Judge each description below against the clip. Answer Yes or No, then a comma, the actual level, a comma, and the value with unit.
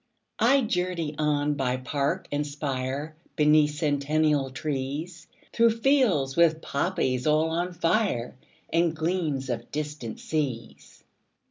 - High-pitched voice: No, medium, 150 Hz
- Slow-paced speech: Yes, slow, 120 wpm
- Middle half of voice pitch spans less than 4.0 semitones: Yes, average, 3.3 semitones